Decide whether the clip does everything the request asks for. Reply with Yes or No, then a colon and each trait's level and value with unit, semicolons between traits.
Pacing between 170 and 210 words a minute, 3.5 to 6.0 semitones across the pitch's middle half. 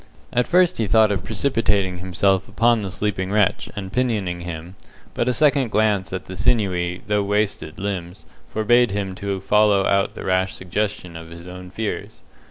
No: average, 175 wpm; average, 2.8 semitones